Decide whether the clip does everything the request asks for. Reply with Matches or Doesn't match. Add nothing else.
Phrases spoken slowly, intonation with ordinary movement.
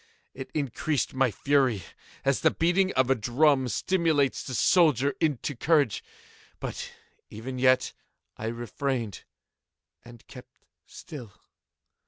Matches